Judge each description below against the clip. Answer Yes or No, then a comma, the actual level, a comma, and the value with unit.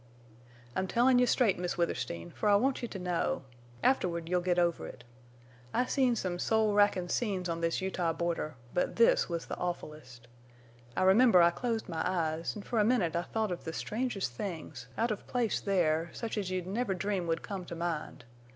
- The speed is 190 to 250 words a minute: Yes, average, 195 wpm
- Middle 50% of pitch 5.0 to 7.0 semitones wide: No, average, 4.3 semitones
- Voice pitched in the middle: Yes, medium, 180 Hz